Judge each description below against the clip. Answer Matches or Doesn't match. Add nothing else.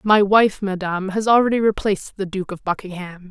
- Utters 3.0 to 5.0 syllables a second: Doesn't match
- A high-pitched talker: Matches